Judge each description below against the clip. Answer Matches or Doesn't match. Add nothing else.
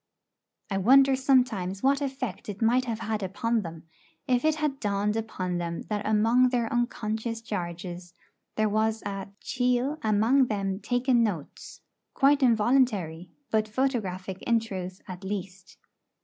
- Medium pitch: Doesn't match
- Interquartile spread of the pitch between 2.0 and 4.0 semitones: Doesn't match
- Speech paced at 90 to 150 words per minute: Matches